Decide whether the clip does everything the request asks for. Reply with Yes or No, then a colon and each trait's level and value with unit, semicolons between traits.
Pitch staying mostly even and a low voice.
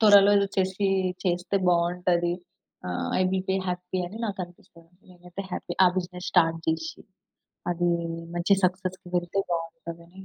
No: narrow, 1.7 semitones; medium, 180 Hz